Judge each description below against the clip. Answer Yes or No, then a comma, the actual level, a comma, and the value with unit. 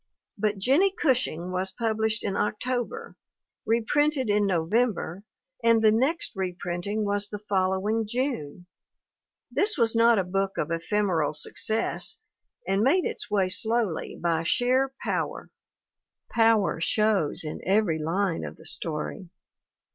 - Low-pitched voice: No, high, 210 Hz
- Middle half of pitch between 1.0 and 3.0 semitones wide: No, average, 4.1 semitones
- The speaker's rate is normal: No, slow, 130 wpm